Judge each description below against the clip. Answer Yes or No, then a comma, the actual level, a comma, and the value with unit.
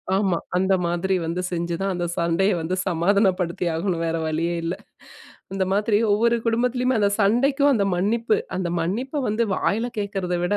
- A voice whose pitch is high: Yes, high, 195 Hz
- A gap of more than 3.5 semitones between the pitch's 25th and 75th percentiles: Yes, average, 4.2 semitones